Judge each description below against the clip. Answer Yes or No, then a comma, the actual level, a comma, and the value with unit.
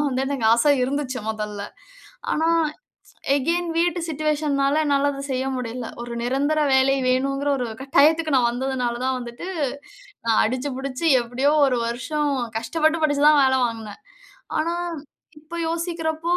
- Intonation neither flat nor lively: Yes, average, 3.5 semitones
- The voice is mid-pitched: No, very high, 275 Hz